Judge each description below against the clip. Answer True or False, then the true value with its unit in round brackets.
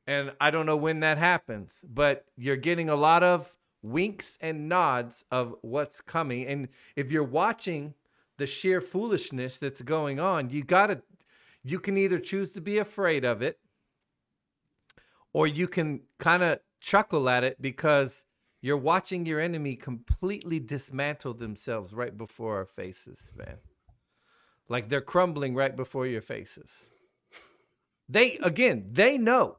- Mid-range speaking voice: True (150 Hz)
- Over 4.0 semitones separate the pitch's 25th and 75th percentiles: True (5.0 semitones)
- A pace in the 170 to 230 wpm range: False (145 wpm)